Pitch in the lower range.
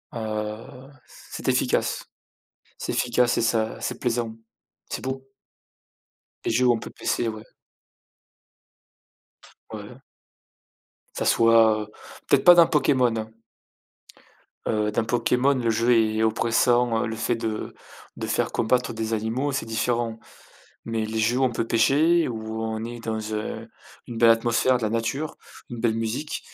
Yes: low, 115 Hz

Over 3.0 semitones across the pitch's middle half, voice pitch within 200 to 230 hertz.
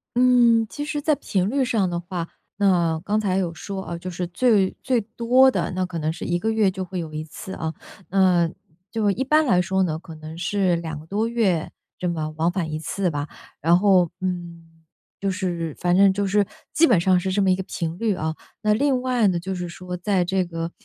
No: average, 3.6 semitones; medium, 185 Hz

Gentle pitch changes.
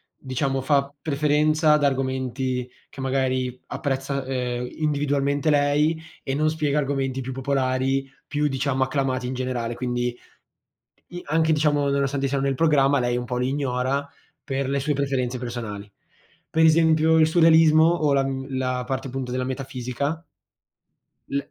Yes: narrow, 2.3 semitones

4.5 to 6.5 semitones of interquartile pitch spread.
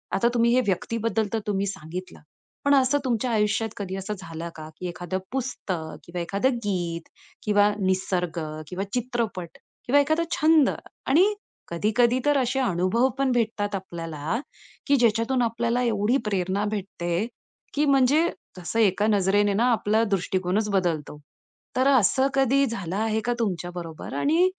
Yes: average, 5.0 semitones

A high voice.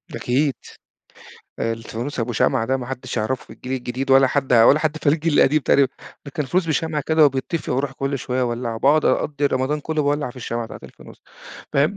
No: low, 135 Hz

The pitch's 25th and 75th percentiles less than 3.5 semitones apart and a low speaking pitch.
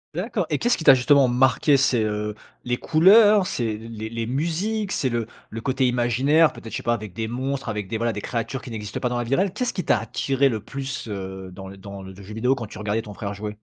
No: average, 4.3 semitones; low, 120 Hz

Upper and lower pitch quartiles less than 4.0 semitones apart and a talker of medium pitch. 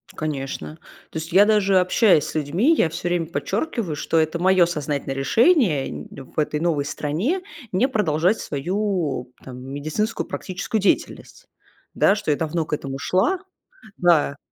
No: average, 5.3 semitones; medium, 165 Hz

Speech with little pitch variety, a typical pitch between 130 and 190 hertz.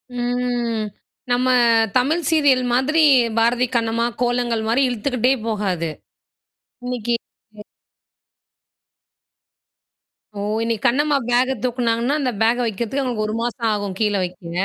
No: narrow, 2.2 semitones; high, 240 Hz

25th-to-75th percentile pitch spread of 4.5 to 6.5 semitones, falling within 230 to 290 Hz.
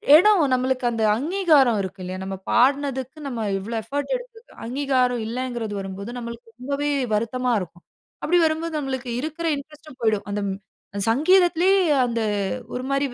Yes: average, 4.9 semitones; very high, 255 Hz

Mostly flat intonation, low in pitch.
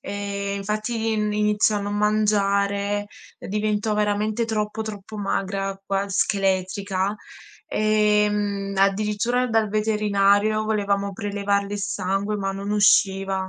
No: narrow, 1.2 semitones; high, 205 Hz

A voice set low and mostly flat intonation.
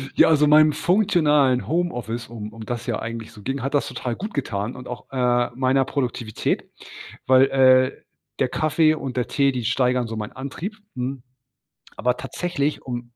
No: low, 130 Hz; average, 3.1 semitones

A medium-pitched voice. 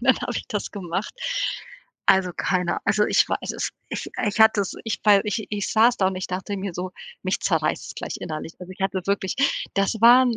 No: high, 200 Hz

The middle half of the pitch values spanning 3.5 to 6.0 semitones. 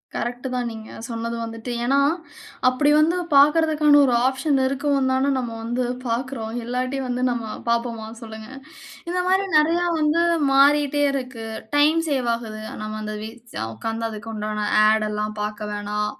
Yes: average, 4.1 semitones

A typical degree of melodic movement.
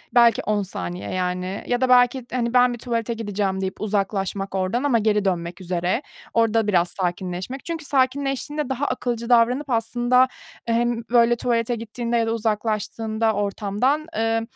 Yes: average, 3.9 semitones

